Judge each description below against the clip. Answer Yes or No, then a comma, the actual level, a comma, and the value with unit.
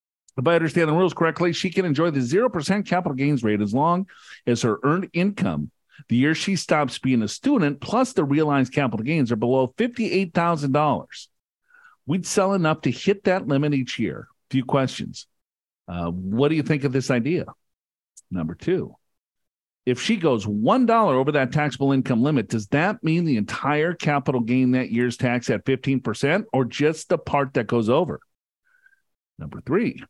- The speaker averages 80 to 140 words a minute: No, average, 170 wpm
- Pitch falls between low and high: Yes, medium, 145 Hz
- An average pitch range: No, wide, 5.7 semitones